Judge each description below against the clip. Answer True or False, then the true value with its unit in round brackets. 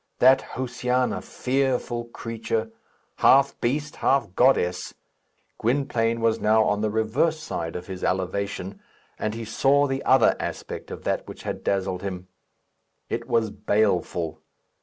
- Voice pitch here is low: True (115 Hz)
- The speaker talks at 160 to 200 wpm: False (135 wpm)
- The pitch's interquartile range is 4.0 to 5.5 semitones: True (4.6 semitones)